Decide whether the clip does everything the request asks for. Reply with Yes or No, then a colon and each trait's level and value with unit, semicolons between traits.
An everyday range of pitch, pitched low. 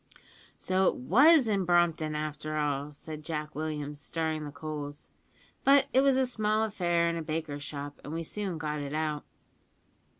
No: average, 3.9 semitones; medium, 155 Hz